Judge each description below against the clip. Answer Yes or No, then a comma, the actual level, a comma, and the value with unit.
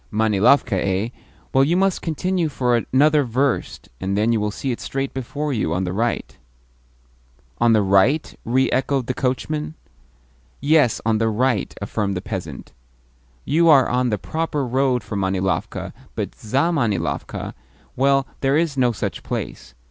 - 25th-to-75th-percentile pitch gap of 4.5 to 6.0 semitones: Yes, average, 5.1 semitones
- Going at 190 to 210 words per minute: No, average, 155 wpm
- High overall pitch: No, low, 125 Hz